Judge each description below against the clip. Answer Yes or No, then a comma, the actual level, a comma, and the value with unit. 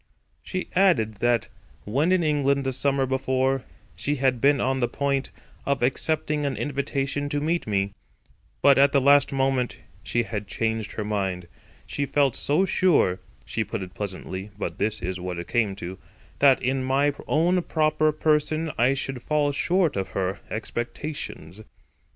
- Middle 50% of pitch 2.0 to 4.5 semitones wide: No, average, 5.1 semitones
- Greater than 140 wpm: Yes, average, 155 wpm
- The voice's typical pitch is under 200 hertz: Yes, low, 135 Hz